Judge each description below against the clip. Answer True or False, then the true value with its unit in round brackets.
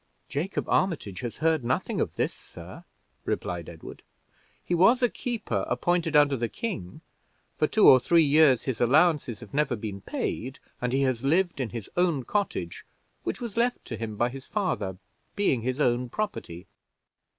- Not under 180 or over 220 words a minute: False (170 wpm)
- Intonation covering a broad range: True (6.8 semitones)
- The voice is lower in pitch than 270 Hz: True (135 Hz)